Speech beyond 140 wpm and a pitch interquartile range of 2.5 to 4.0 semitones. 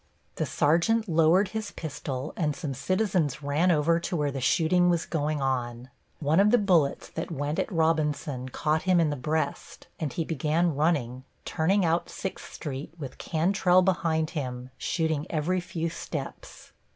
Yes: average, 165 wpm; average, 3.4 semitones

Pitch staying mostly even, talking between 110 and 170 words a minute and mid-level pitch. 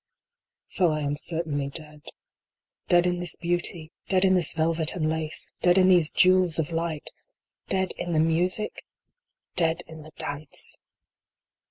Yes: narrow, 2.3 semitones; average, 150 wpm; medium, 165 Hz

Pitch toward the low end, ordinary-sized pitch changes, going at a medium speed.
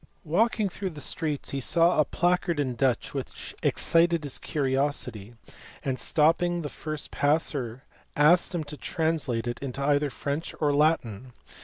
No: medium, 150 Hz; average, 3.7 semitones; average, 150 wpm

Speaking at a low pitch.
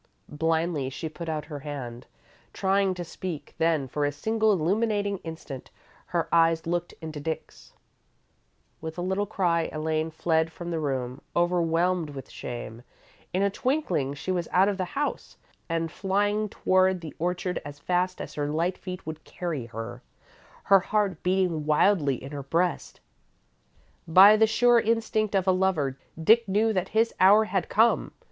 No: medium, 175 Hz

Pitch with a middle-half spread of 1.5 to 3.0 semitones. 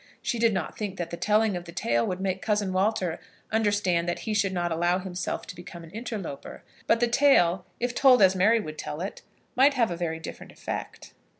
No: average, 4.1 semitones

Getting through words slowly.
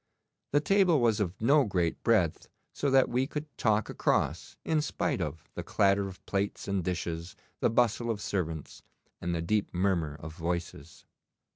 No: average, 165 wpm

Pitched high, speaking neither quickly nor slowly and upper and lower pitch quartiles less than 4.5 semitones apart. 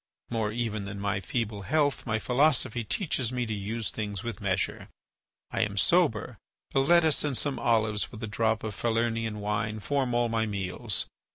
No: low, 115 Hz; average, 175 wpm; average, 2.7 semitones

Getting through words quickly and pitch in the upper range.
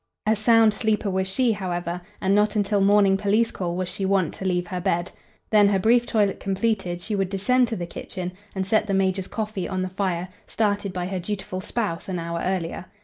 Yes: fast, 210 wpm; high, 195 Hz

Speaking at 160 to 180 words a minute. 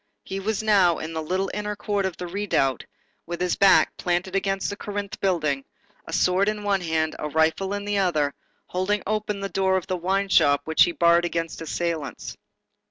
No: average, 195 wpm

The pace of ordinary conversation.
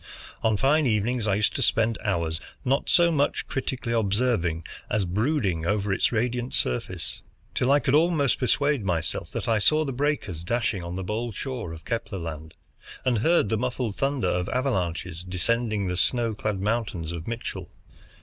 Yes: average, 170 wpm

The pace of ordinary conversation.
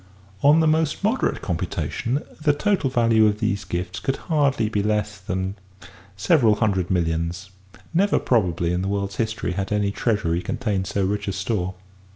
Yes: average, 165 wpm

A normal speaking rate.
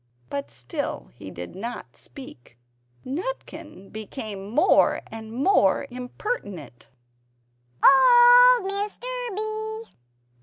No: slow, 85 wpm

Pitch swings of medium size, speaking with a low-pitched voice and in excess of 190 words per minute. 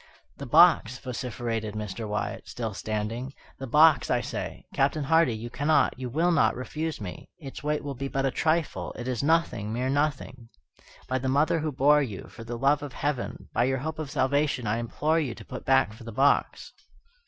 Yes: average, 4.2 semitones; low, 130 Hz; average, 200 wpm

